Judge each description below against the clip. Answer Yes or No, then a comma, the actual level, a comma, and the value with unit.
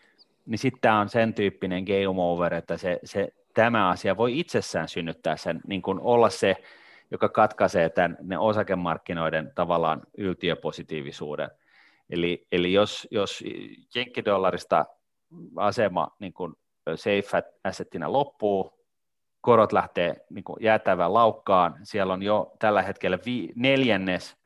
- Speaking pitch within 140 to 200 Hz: No, very low, 95 Hz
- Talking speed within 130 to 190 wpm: No, average, 120 wpm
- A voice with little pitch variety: No, average, 3.9 semitones